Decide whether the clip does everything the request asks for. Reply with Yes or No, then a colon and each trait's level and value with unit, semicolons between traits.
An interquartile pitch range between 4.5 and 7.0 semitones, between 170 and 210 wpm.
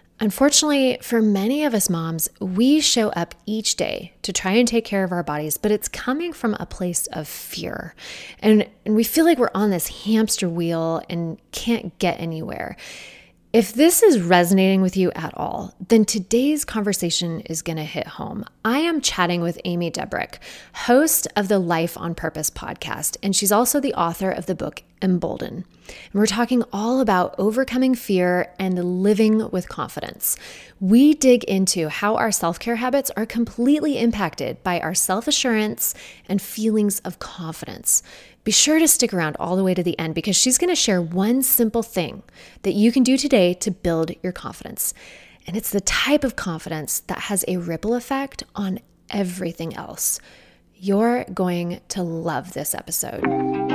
Yes: average, 5.0 semitones; average, 175 wpm